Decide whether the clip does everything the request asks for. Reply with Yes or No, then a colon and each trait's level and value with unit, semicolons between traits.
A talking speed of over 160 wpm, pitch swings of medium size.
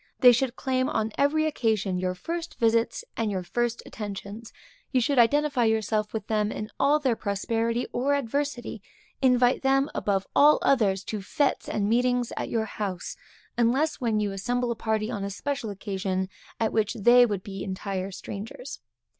Yes: average, 170 wpm; average, 3.8 semitones